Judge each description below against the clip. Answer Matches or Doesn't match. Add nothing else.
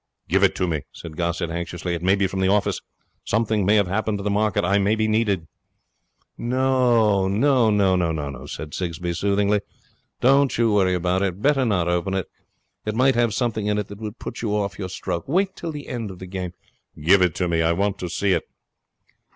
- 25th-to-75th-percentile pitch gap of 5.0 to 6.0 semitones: Doesn't match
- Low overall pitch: Matches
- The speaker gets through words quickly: Matches